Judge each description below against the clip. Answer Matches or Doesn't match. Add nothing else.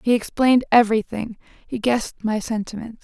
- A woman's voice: Matches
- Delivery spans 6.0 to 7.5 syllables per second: Matches